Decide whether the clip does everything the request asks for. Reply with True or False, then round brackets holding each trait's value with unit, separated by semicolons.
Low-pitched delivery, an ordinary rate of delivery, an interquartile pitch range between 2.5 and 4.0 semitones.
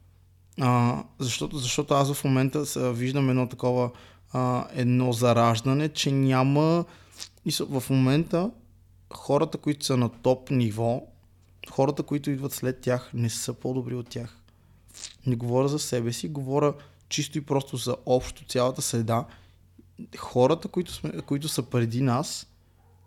True (125 Hz; 140 wpm; 3.3 semitones)